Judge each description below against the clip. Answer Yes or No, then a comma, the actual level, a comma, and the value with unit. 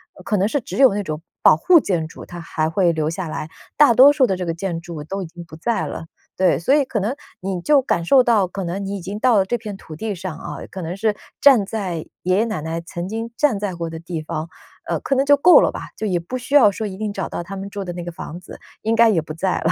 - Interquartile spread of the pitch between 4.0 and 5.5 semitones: Yes, average, 4.8 semitones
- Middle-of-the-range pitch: No, high, 195 Hz